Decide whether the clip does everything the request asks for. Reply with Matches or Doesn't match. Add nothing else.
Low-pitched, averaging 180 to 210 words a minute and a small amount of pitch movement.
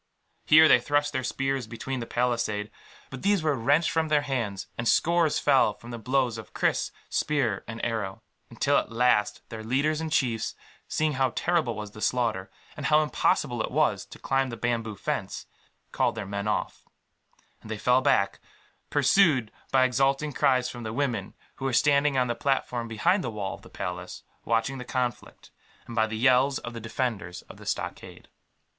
Doesn't match